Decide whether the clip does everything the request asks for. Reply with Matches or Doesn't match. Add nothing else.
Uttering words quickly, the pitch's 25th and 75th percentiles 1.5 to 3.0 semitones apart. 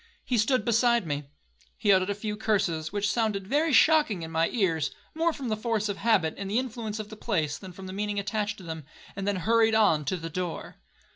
Doesn't match